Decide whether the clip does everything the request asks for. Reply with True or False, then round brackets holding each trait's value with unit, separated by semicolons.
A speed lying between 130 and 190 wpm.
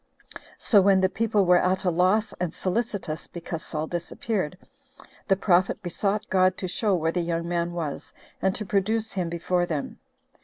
True (170 wpm)